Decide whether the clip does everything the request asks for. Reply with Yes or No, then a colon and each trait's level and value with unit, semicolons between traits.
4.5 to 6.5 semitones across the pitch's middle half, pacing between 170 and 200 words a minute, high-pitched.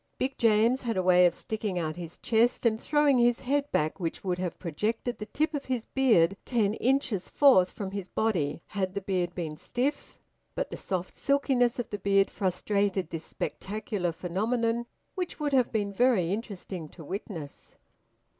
Yes: average, 5.1 semitones; average, 175 wpm; high, 205 Hz